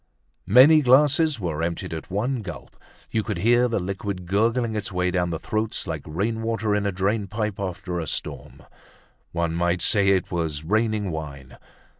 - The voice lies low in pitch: Yes, low, 100 Hz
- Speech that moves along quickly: No, average, 165 wpm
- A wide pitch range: No, average, 4.5 semitones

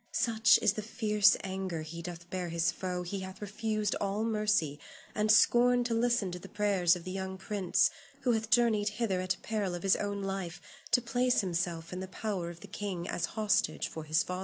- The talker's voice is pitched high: Yes, high, 195 Hz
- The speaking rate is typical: No, fast, 210 wpm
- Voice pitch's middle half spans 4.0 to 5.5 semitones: No, average, 3.3 semitones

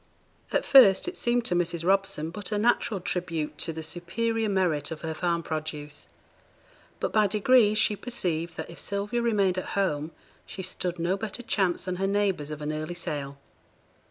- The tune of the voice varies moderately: Yes, average, 4.2 semitones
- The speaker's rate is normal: Yes, average, 180 wpm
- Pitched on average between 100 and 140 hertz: No, medium, 185 Hz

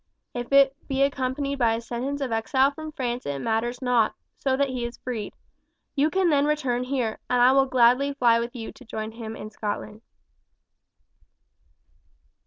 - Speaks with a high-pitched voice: Yes, very high, 250 Hz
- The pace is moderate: Yes, average, 175 wpm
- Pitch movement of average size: Yes, average, 3.0 semitones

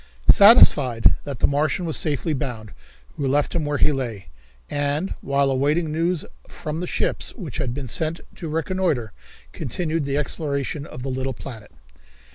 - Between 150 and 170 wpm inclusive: Yes, average, 160 wpm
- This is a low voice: No, medium, 145 Hz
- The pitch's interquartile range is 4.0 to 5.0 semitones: No, average, 3.3 semitones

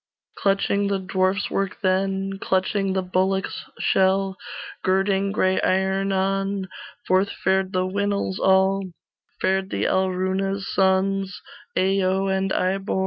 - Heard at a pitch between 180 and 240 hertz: Yes, high, 190 Hz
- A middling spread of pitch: No, narrow, 0.6 semitones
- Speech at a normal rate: No, slow, 115 wpm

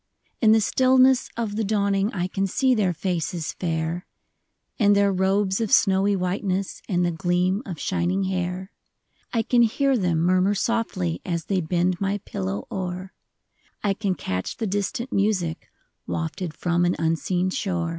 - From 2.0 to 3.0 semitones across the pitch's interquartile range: Yes, narrow, 2.6 semitones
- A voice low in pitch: No, high, 190 Hz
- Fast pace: No, average, 155 wpm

